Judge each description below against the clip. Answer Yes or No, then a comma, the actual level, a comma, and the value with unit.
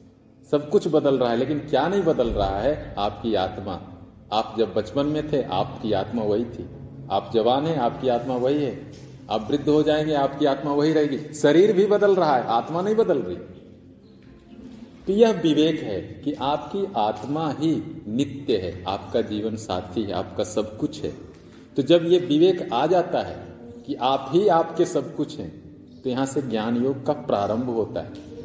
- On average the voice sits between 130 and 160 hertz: Yes, medium, 140 Hz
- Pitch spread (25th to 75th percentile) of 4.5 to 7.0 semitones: Yes, average, 5.1 semitones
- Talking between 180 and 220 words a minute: Yes, fast, 190 wpm